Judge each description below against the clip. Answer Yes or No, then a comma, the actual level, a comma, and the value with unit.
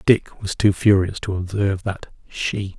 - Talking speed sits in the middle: Yes, average, 170 wpm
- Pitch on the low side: Yes, very low, 95 Hz